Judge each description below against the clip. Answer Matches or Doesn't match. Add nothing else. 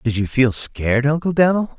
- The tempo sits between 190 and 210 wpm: Matches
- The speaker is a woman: Doesn't match